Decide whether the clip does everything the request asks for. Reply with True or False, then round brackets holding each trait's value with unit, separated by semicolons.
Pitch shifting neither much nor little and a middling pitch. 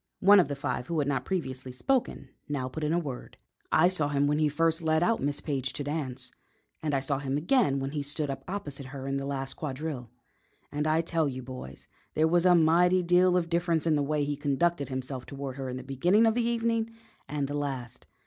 True (3.8 semitones; 145 Hz)